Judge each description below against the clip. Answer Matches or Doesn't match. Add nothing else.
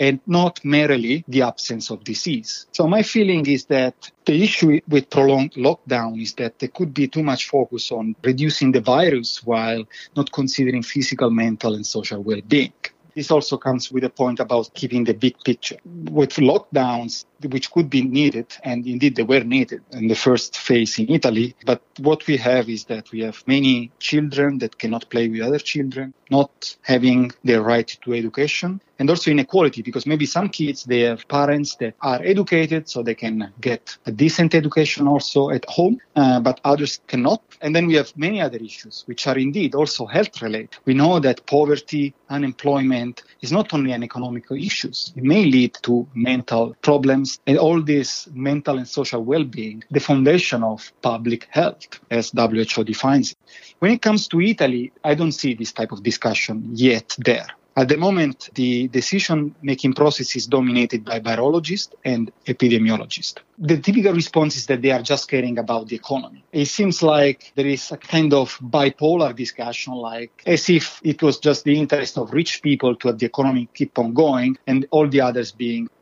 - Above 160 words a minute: Matches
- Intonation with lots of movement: Doesn't match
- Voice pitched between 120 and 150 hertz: Matches